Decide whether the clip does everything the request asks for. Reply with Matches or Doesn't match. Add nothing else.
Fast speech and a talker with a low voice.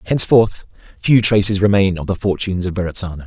Doesn't match